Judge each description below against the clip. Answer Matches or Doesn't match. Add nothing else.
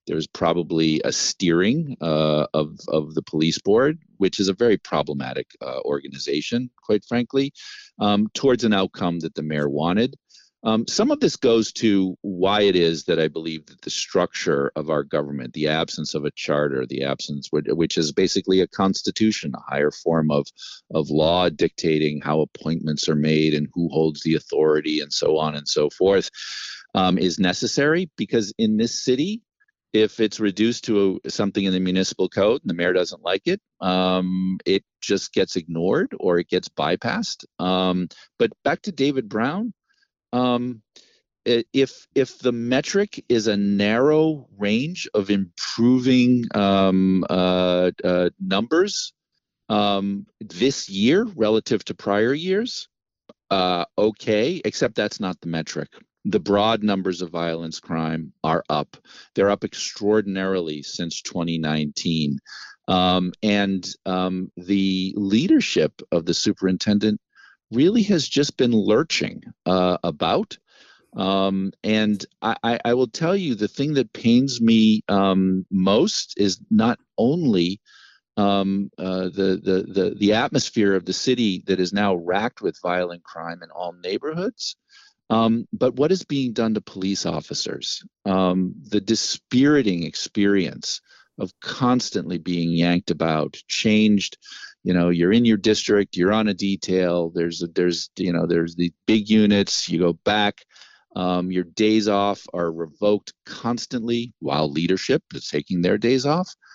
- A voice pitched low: Matches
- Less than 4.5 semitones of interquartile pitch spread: Doesn't match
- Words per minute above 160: Doesn't match